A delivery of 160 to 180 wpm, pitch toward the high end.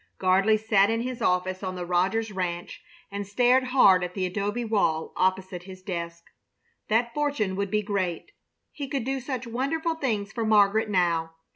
Yes: average, 170 wpm; high, 200 Hz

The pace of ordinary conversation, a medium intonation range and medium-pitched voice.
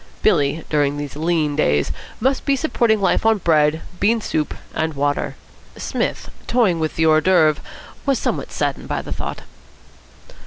No: average, 155 wpm; wide, 6.4 semitones; medium, 160 Hz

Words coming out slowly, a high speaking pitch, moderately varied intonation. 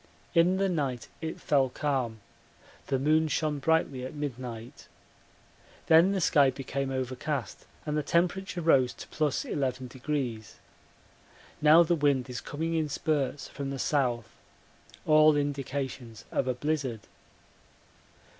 No: slow, 125 wpm; medium, 140 Hz; average, 3.3 semitones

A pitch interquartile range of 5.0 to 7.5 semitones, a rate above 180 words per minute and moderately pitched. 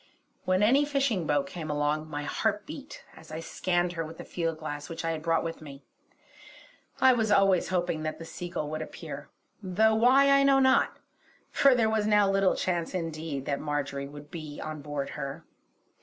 Yes: wide, 5.6 semitones; average, 190 wpm; medium, 165 Hz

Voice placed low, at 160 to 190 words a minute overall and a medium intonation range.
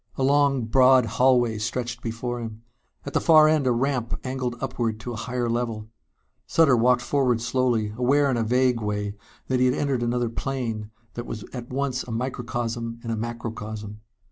No: low, 120 Hz; average, 180 wpm; narrow, 2.1 semitones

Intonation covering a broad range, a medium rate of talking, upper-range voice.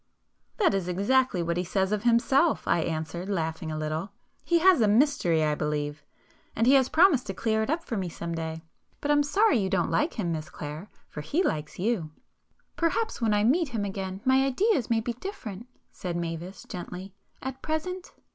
Yes: wide, 7.8 semitones; average, 175 wpm; high, 205 Hz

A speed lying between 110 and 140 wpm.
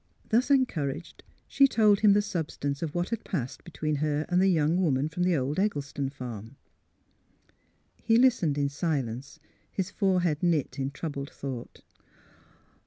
No: average, 150 wpm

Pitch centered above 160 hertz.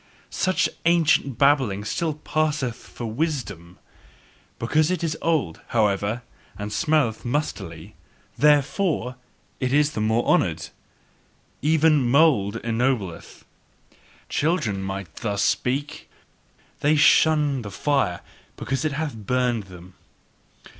No: low, 125 Hz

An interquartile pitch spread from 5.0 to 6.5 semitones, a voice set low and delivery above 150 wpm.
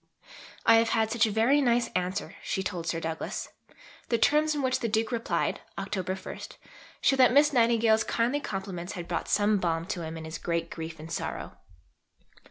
No: wide, 5.5 semitones; high, 210 Hz; average, 185 wpm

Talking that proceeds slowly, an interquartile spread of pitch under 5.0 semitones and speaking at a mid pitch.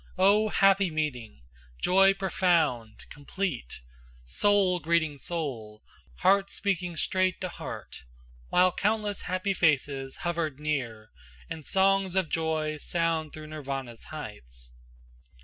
No: slow, 110 wpm; wide, 5.6 semitones; medium, 160 Hz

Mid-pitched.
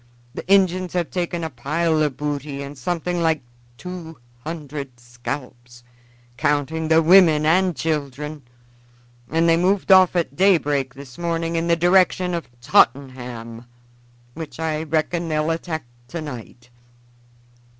Yes: medium, 160 Hz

